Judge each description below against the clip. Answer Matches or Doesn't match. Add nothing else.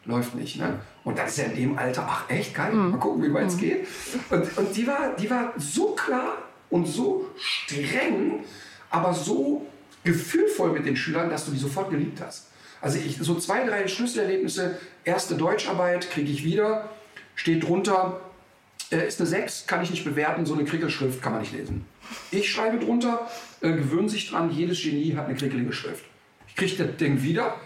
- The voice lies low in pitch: Doesn't match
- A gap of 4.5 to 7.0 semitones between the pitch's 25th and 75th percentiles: Matches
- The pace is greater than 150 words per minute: Matches